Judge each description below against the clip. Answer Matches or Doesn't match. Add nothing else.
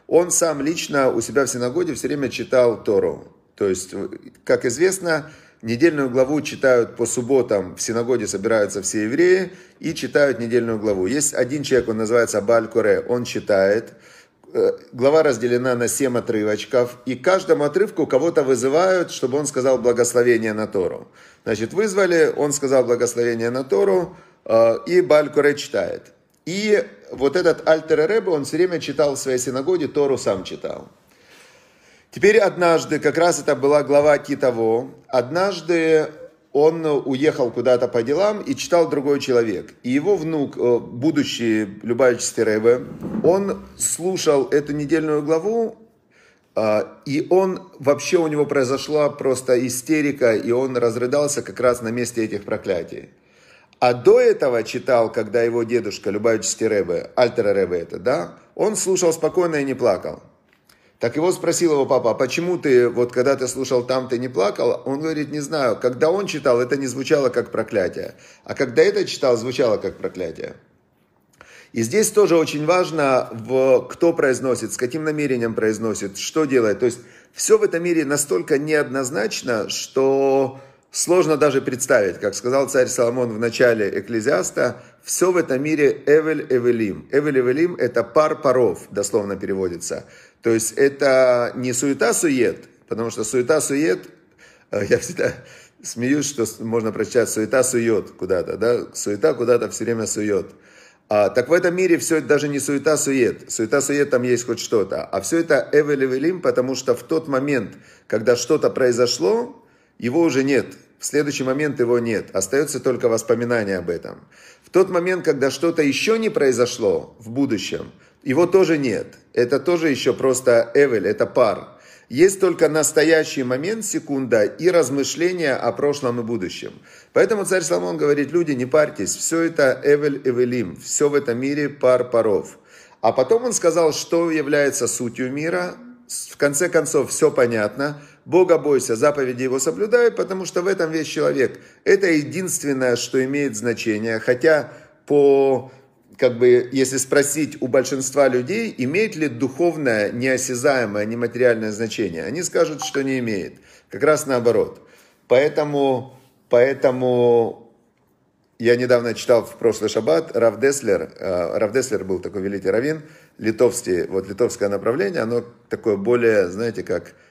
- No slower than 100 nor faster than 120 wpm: Doesn't match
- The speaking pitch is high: Doesn't match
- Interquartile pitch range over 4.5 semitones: Matches